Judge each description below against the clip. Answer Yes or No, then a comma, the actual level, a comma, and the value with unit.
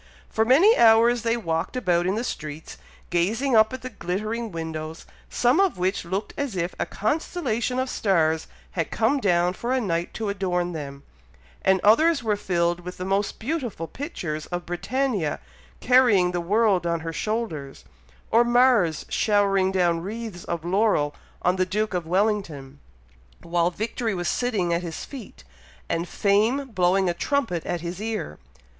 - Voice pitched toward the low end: No, high, 195 Hz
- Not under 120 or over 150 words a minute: No, average, 165 wpm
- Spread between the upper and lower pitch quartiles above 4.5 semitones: Yes, average, 5.1 semitones